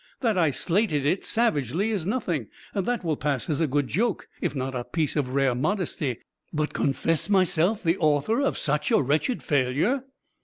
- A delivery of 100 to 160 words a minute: No, average, 180 wpm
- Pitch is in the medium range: Yes, medium, 155 Hz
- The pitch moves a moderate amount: No, wide, 6.0 semitones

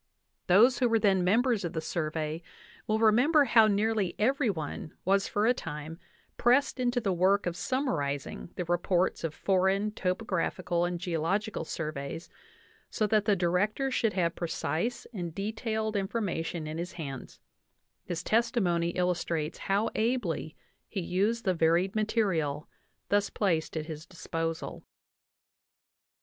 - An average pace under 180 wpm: Yes, average, 140 wpm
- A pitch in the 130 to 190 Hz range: Yes, medium, 185 Hz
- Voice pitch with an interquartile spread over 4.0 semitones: Yes, average, 4.6 semitones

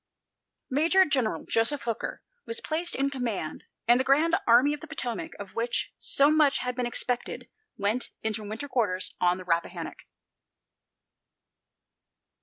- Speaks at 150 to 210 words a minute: No, average, 140 wpm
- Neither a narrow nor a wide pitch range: Yes, average, 4.9 semitones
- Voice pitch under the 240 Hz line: No, very high, 250 Hz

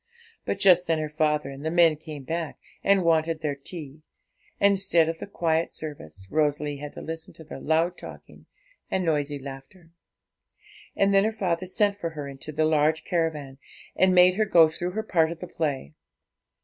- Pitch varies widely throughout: No, average, 3.1 semitones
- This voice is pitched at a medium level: Yes, medium, 160 Hz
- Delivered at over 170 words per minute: Yes, average, 190 wpm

